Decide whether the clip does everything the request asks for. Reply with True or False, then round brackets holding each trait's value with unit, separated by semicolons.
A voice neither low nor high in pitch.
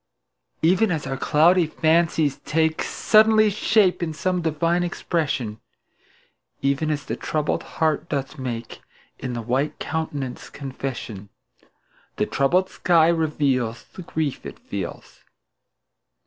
True (155 Hz)